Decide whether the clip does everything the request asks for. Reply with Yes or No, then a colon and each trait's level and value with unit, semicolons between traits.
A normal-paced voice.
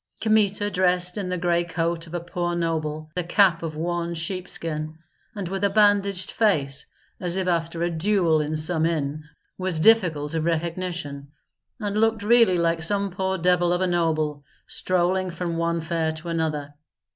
Yes: average, 170 wpm